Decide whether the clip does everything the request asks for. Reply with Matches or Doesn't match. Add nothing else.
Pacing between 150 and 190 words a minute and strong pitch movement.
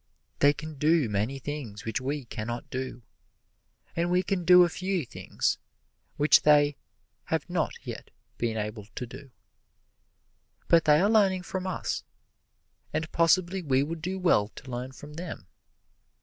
Matches